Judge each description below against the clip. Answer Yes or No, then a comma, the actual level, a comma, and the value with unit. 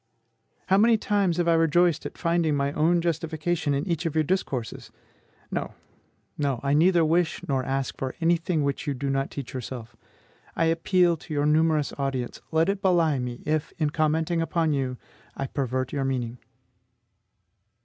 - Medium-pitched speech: Yes, medium, 155 Hz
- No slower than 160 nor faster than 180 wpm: Yes, average, 170 wpm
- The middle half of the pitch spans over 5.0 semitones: No, average, 3.7 semitones